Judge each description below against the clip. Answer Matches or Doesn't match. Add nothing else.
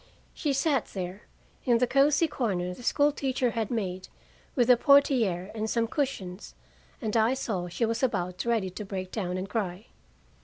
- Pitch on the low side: Doesn't match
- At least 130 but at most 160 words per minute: Doesn't match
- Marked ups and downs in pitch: Matches